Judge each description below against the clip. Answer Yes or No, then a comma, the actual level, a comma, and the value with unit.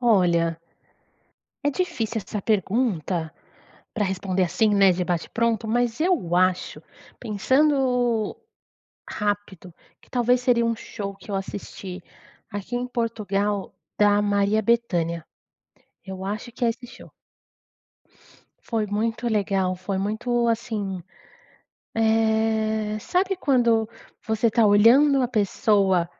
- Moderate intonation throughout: Yes, average, 3.3 semitones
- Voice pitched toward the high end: Yes, high, 215 Hz